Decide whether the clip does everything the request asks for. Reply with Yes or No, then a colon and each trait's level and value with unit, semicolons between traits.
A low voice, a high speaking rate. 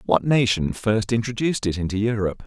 No: low, 110 Hz; average, 170 wpm